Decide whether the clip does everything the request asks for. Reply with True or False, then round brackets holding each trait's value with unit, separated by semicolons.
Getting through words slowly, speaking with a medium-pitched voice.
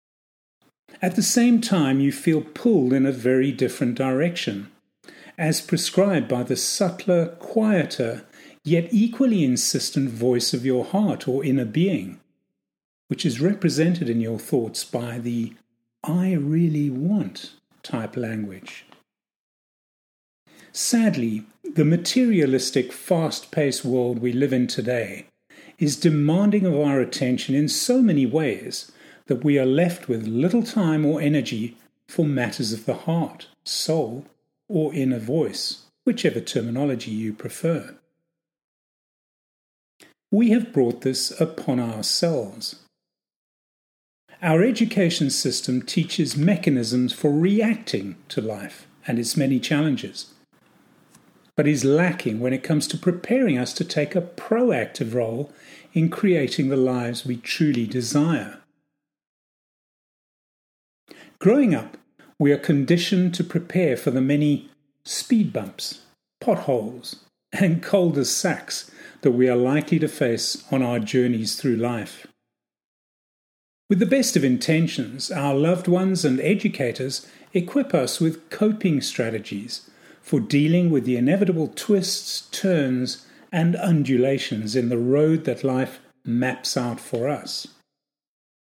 True (125 wpm; 145 Hz)